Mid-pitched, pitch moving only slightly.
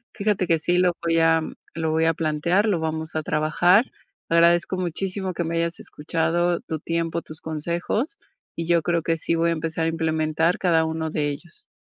Yes: medium, 165 Hz; narrow, 1.4 semitones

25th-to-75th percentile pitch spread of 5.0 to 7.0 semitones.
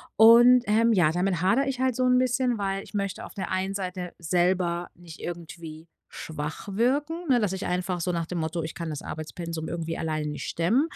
Yes: wide, 5.5 semitones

